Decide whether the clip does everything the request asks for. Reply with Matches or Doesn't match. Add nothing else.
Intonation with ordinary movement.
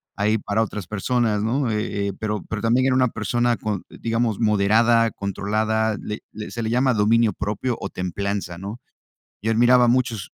Doesn't match